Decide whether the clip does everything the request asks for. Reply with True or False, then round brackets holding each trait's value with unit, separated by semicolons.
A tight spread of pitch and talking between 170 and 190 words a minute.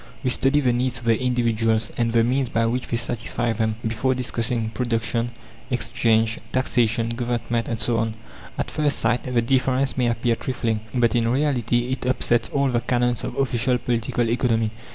True (1.7 semitones; 175 wpm)